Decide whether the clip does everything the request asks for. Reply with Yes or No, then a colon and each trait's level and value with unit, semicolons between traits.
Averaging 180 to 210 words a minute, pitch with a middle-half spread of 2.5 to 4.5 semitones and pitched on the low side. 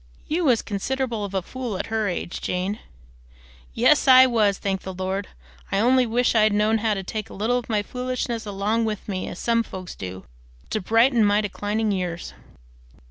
No: average, 190 wpm; average, 3.2 semitones; high, 215 Hz